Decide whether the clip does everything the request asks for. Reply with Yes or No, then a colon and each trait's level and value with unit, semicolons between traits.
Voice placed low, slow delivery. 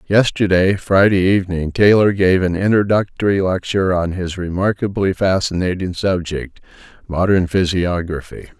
Yes: very low, 95 Hz; slow, 100 wpm